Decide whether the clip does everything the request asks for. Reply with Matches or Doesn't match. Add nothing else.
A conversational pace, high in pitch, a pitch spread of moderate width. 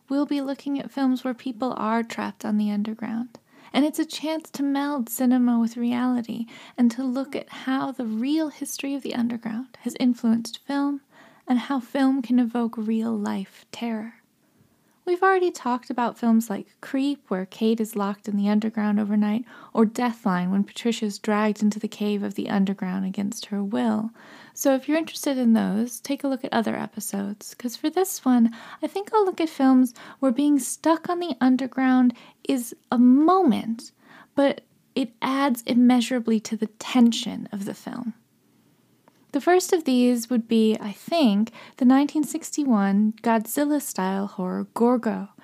Matches